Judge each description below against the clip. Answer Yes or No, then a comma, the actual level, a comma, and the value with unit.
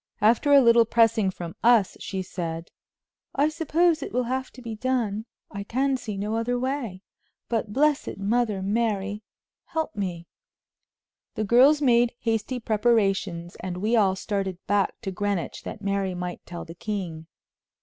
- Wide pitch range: No, average, 4.0 semitones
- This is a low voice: No, high, 215 Hz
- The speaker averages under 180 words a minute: Yes, average, 155 wpm